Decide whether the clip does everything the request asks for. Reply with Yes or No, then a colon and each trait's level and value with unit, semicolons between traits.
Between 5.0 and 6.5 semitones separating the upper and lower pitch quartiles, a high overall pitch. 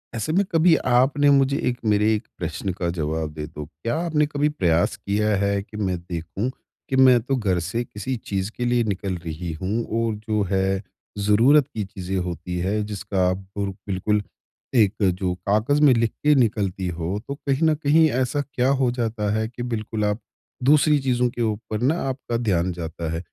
No: wide, 5.4 semitones; low, 105 Hz